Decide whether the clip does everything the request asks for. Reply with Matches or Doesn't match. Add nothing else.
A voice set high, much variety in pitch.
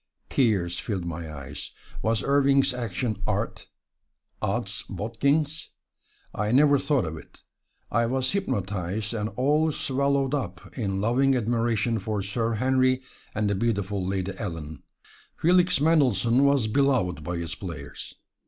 Doesn't match